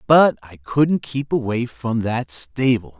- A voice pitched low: Yes, low, 120 Hz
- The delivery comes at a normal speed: Yes, average, 160 wpm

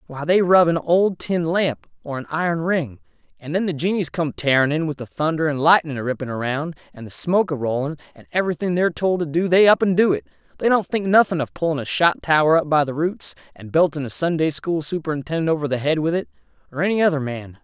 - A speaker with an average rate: No, fast, 240 wpm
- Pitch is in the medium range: Yes, medium, 155 Hz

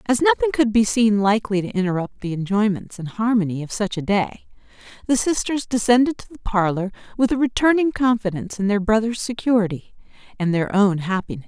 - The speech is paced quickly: No, average, 180 wpm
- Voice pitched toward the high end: Yes, high, 215 Hz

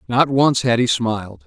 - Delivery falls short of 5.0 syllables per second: Yes, 4.7 syllables/s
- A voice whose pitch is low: Yes, low, 120 Hz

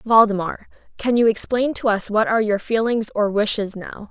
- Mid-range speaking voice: No, high, 215 Hz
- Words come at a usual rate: Yes, average, 190 wpm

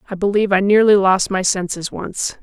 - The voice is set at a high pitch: Yes, high, 195 Hz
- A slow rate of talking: No, average, 200 wpm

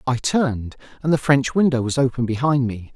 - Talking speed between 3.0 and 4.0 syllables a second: No, 5.5 syllables/s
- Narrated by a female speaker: No, male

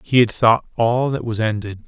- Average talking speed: No, fast, 225 wpm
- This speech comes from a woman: No, male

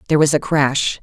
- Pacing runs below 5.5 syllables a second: No, 6.1 syllables/s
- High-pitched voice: No, medium, 145 Hz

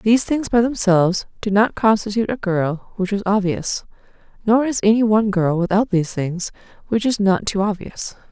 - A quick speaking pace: No, average, 180 wpm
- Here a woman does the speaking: Yes, female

